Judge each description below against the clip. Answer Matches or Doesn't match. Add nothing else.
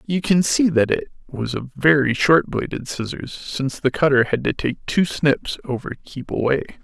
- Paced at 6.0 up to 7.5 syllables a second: Doesn't match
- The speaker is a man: Matches